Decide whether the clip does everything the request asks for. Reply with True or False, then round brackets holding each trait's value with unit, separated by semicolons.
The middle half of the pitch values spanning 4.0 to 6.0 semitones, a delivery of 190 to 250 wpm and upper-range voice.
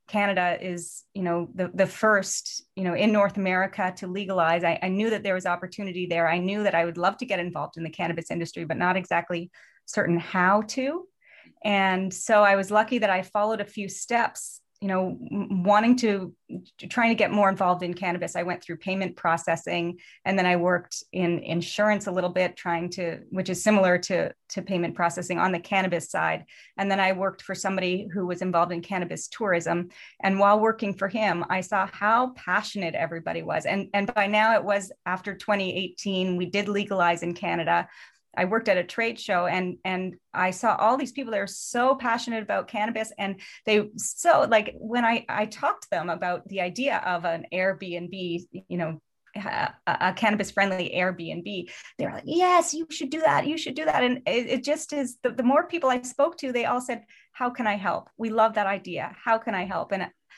False (3.6 semitones; 205 wpm; 195 Hz)